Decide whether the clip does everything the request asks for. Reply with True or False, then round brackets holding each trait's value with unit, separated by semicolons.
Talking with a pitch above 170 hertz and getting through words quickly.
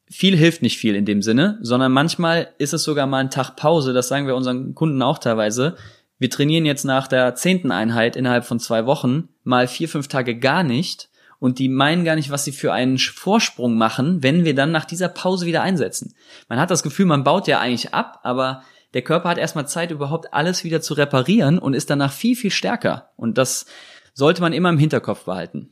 False (140 Hz; 215 wpm)